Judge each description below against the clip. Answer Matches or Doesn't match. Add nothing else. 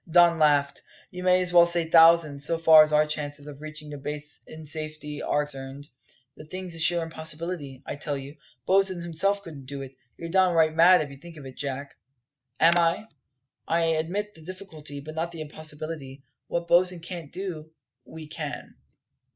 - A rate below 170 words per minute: Doesn't match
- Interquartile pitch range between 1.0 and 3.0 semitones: Matches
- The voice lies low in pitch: Doesn't match